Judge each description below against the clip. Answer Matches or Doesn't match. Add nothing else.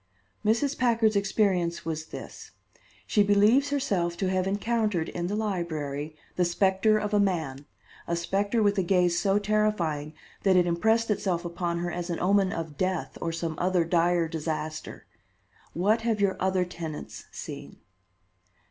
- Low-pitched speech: Doesn't match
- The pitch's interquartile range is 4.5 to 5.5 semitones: Doesn't match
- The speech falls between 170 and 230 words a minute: Doesn't match